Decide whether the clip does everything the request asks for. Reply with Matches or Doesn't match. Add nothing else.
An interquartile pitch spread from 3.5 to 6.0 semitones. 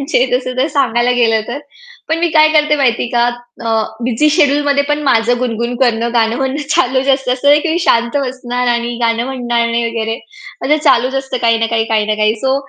Doesn't match